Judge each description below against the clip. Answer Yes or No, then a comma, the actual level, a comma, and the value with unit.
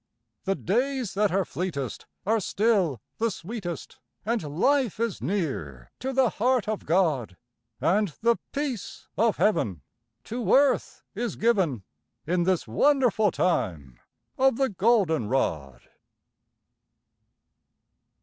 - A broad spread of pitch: Yes, wide, 7.0 semitones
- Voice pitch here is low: No, high, 195 Hz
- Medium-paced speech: No, slow, 115 wpm